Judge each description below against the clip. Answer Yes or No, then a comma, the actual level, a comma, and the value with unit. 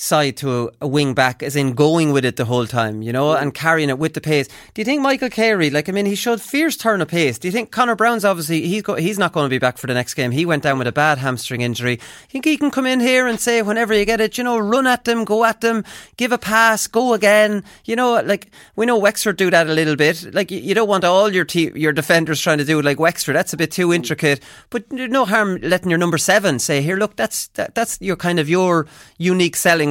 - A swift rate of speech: Yes, fast, 275 wpm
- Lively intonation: Yes, wide, 6.8 semitones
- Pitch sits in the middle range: Yes, medium, 180 Hz